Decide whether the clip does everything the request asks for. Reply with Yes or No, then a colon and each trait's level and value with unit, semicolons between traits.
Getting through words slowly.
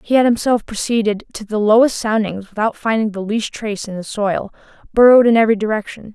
No: average, 195 wpm